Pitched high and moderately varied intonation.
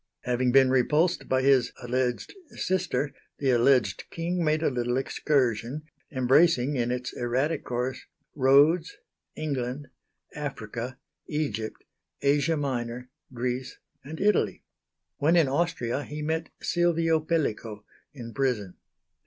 No: low, 135 Hz; average, 4.0 semitones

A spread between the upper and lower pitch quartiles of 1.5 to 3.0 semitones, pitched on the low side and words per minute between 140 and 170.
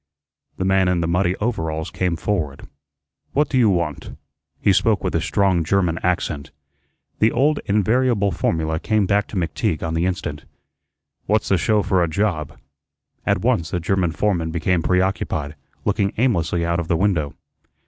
No: average, 3.8 semitones; very low, 90 Hz; average, 160 wpm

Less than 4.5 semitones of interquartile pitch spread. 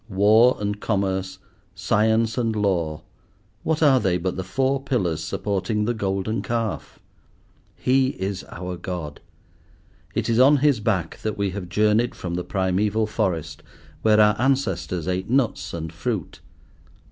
Yes: average, 3.7 semitones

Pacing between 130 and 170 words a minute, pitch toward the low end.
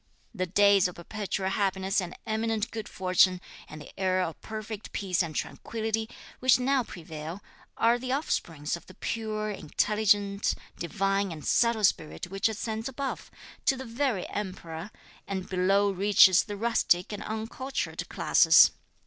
No: average, 145 wpm; high, 200 Hz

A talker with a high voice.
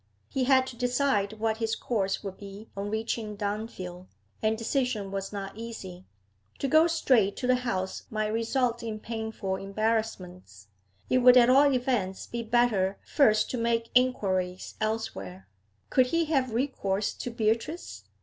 Yes: high, 220 Hz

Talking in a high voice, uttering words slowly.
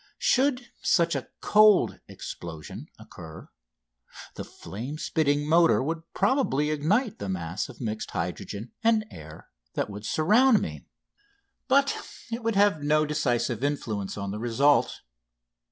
No: medium, 150 Hz; slow, 130 wpm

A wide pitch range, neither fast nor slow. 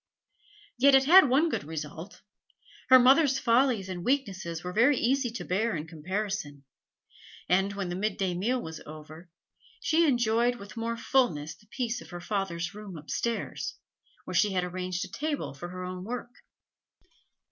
Yes: wide, 5.8 semitones; average, 160 wpm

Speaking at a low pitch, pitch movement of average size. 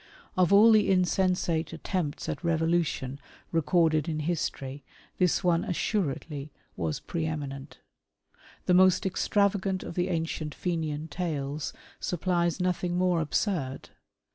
No: medium, 170 Hz; average, 3.2 semitones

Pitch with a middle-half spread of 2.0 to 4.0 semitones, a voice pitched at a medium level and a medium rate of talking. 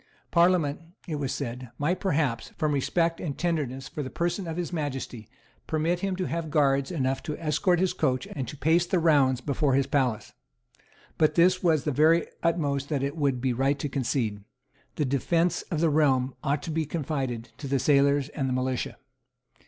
Yes: average, 3.7 semitones; medium, 145 Hz; average, 190 wpm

